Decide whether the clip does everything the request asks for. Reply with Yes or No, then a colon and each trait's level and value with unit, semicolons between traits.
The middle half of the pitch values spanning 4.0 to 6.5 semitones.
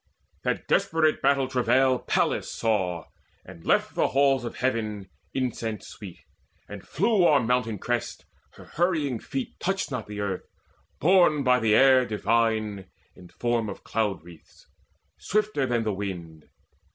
Yes: average, 4.7 semitones